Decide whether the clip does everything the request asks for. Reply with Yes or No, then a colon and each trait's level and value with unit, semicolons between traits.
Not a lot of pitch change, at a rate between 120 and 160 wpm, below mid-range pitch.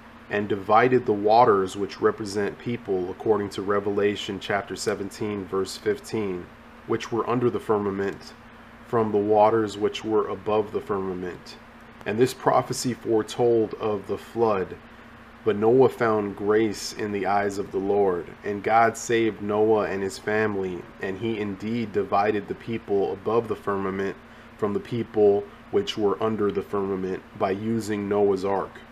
Yes: narrow, 2.0 semitones; average, 150 wpm; low, 105 Hz